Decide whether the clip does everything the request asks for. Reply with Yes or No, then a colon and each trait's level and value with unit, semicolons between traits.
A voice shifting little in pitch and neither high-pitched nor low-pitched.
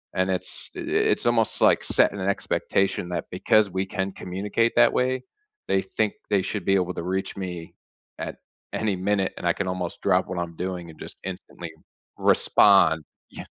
No: narrow, 2.2 semitones; very low, 95 Hz